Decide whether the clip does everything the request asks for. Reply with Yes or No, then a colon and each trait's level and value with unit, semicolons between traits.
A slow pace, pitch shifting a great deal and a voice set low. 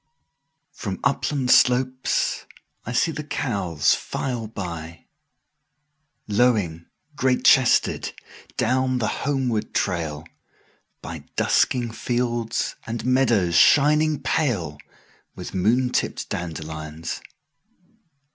Yes: slow, 80 wpm; wide, 6.7 semitones; low, 120 Hz